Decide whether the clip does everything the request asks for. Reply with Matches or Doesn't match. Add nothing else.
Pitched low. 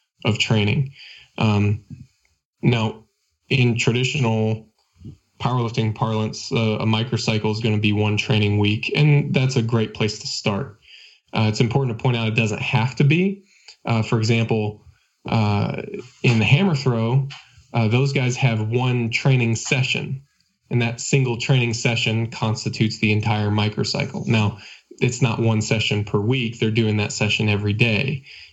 Matches